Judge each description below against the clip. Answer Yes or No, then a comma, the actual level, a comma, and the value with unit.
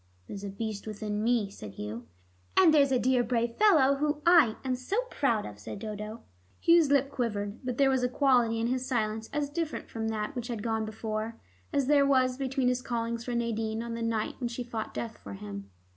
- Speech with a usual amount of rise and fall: Yes, average, 3.5 semitones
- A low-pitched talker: No, high, 235 Hz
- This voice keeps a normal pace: No, fast, 215 wpm